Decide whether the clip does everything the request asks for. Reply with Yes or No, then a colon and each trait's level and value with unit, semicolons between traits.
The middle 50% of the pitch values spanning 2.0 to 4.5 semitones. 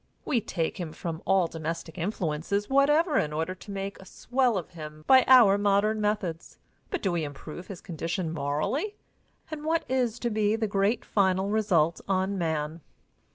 No: average, 4.9 semitones